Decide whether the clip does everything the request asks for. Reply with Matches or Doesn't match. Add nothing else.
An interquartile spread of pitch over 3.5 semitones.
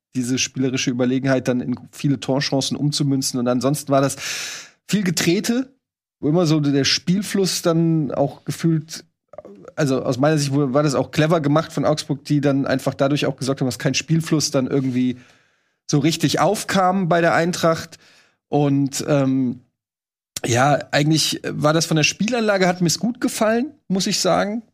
Matches